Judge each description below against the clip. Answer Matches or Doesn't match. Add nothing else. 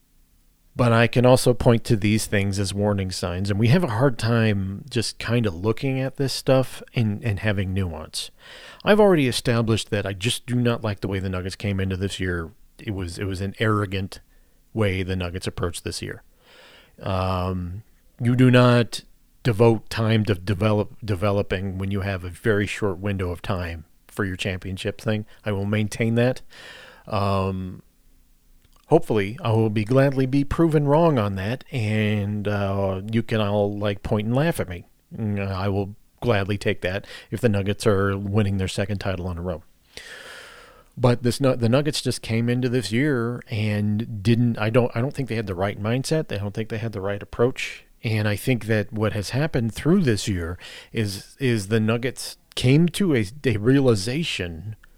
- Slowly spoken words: Doesn't match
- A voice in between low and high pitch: Doesn't match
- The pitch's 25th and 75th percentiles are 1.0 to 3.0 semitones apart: Doesn't match